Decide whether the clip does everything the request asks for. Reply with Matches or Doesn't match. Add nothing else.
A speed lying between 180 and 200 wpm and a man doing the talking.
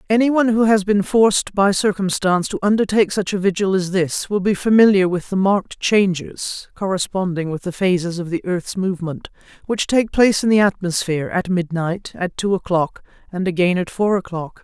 Doesn't match